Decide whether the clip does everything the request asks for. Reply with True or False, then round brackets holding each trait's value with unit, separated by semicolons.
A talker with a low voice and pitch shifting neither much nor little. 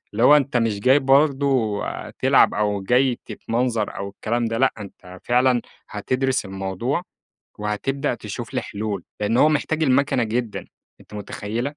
True (120 Hz; 4.2 semitones)